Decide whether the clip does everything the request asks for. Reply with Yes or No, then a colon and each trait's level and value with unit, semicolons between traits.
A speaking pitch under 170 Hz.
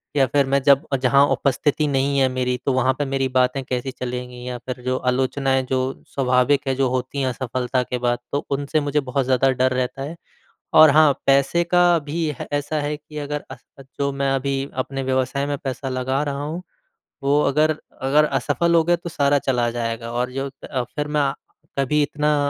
Yes: low, 135 Hz